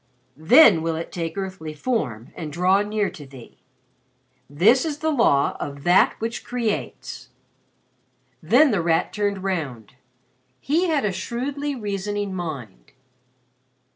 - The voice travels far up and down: Yes, wide, 7.0 semitones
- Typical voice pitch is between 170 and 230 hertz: Yes, high, 190 Hz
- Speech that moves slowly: Yes, slow, 130 wpm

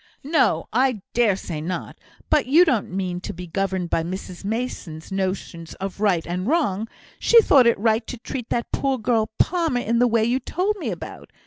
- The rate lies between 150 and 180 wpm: No, average, 195 wpm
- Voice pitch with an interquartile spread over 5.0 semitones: Yes, wide, 5.4 semitones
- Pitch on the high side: Yes, high, 220 Hz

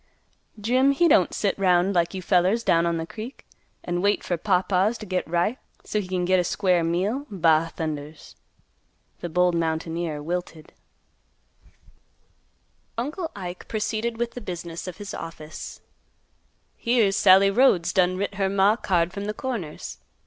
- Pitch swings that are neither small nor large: Yes, average, 3.7 semitones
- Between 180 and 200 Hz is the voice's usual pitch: Yes, medium, 185 Hz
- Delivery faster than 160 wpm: No, average, 155 wpm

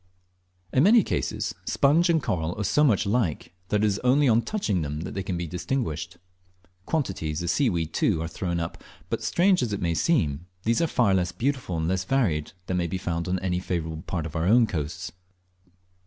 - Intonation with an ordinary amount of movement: No, wide, 6.8 semitones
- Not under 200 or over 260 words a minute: Yes, fast, 205 wpm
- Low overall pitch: Yes, very low, 95 Hz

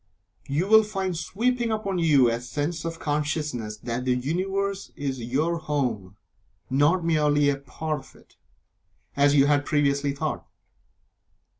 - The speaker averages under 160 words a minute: Yes, average, 140 wpm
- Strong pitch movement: No, average, 3.7 semitones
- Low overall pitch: No, medium, 150 Hz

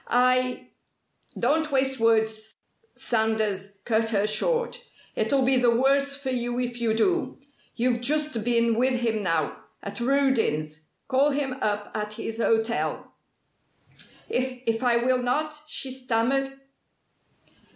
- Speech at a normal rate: No, slow, 130 wpm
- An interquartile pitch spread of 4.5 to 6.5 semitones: No, average, 3.2 semitones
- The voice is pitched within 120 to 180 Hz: No, high, 245 Hz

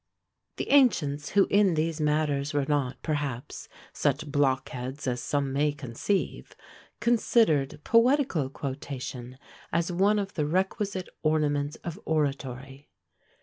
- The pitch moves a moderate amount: Yes, average, 4.8 semitones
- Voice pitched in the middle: Yes, medium, 150 Hz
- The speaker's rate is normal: No, slow, 115 wpm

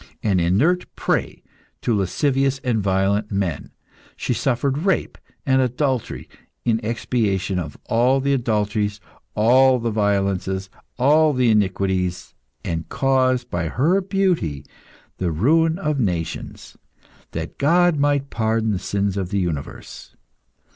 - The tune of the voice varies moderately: No, wide, 5.8 semitones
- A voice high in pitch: No, low, 115 Hz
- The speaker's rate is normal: No, slow, 125 wpm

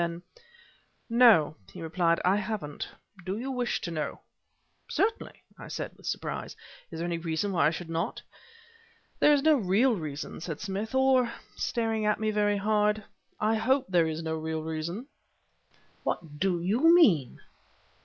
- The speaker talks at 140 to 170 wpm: Yes, average, 160 wpm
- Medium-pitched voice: No, high, 195 Hz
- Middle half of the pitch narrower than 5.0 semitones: No, wide, 5.6 semitones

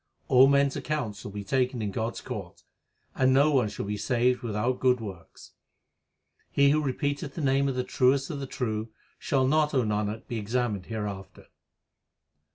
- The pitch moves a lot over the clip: No, average, 4.3 semitones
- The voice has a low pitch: Yes, low, 125 Hz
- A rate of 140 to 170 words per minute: No, average, 180 wpm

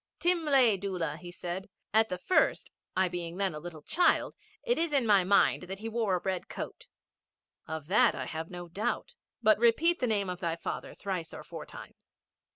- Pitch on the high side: Yes, high, 195 Hz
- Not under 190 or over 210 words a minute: Yes, average, 195 wpm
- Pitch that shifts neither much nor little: Yes, average, 4.5 semitones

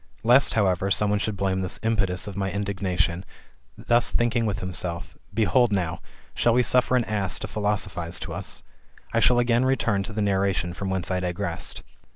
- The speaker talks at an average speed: Yes, average, 185 wpm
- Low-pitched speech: Yes, low, 100 Hz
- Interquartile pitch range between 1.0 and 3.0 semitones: No, average, 3.5 semitones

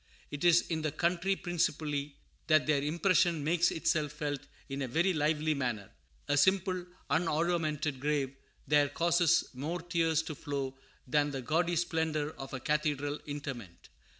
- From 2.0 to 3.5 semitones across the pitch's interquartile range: Yes, average, 2.9 semitones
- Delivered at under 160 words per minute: Yes, average, 150 wpm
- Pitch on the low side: No, medium, 150 Hz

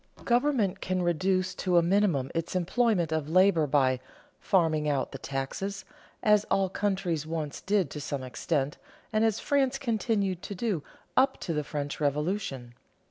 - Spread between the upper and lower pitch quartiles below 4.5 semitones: No, average, 5.3 semitones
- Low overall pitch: No, medium, 180 Hz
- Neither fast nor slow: Yes, average, 155 wpm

